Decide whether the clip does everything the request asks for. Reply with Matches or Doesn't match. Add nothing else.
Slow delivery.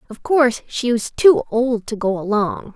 Doesn't match